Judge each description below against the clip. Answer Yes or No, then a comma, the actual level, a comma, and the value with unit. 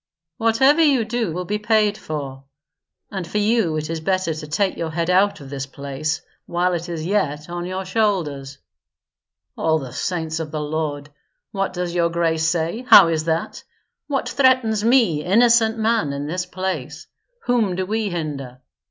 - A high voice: No, medium, 175 Hz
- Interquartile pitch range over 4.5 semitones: Yes, average, 5.3 semitones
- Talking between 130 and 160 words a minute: No, average, 170 wpm